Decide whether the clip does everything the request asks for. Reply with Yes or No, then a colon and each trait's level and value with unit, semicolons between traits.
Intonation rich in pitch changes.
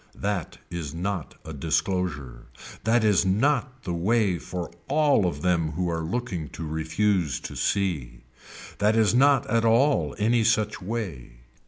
Yes: wide, 6.0 semitones